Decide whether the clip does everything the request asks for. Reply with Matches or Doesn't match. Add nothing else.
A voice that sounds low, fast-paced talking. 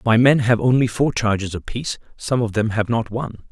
Matches